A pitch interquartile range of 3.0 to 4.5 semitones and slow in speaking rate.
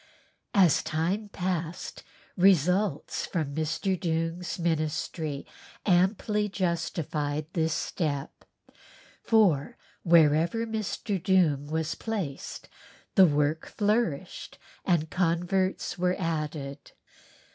Yes: average, 3.4 semitones; slow, 85 wpm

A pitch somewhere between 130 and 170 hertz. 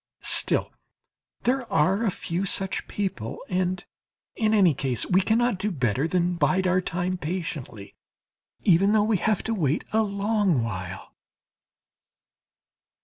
No: medium, 185 Hz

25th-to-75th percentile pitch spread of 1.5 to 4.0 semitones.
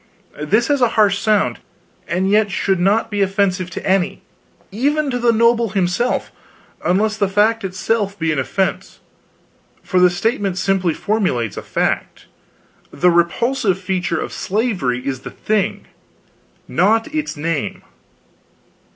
Yes: average, 3.7 semitones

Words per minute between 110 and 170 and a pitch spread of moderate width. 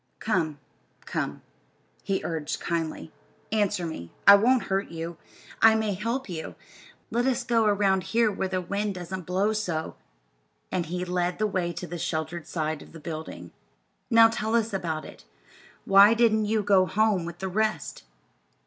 Yes: average, 165 wpm; average, 4.1 semitones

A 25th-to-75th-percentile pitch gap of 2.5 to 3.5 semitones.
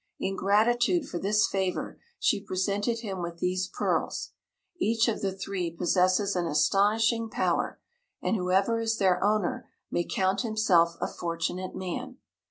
Yes: average, 3.1 semitones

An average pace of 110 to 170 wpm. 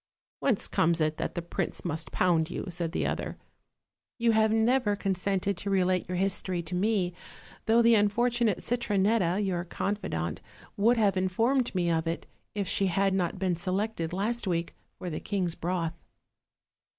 Yes: average, 165 wpm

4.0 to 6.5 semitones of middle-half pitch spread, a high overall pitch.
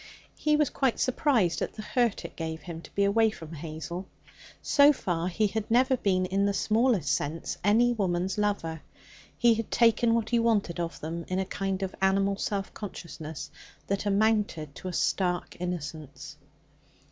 Yes: average, 4.7 semitones; high, 195 Hz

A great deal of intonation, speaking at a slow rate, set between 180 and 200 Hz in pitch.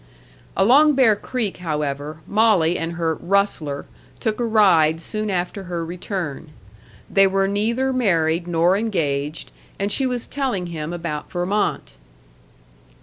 No: average, 4.7 semitones; slow, 130 wpm; medium, 185 Hz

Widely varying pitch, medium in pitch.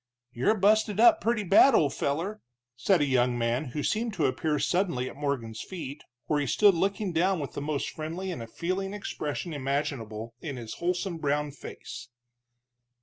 Yes: wide, 6.2 semitones; medium, 155 Hz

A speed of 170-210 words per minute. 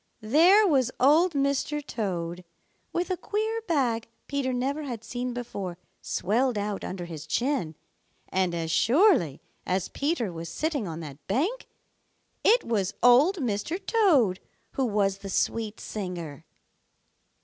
No: slow, 135 wpm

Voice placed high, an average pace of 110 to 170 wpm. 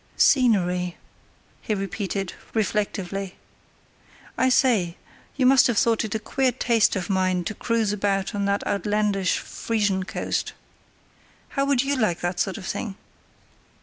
Yes: high, 205 Hz; average, 140 wpm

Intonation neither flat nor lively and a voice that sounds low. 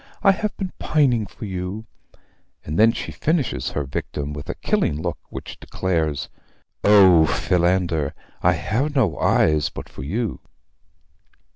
No: wide, 6.6 semitones; very low, 90 Hz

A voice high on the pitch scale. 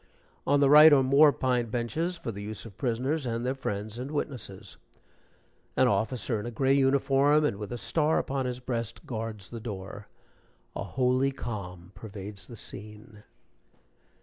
No: low, 120 Hz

